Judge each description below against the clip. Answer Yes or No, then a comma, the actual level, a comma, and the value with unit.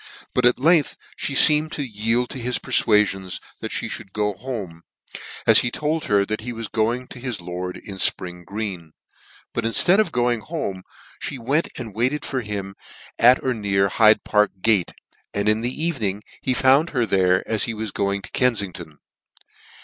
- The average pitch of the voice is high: No, low, 110 Hz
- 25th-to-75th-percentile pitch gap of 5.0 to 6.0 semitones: No, average, 4.3 semitones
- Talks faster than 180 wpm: Yes, average, 190 wpm